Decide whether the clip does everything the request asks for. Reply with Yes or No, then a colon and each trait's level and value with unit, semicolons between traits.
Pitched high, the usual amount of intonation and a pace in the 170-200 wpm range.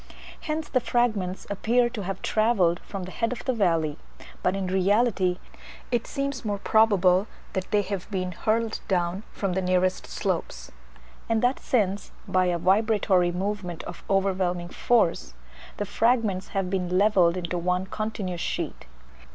No: high, 195 Hz; average, 3.3 semitones; average, 150 wpm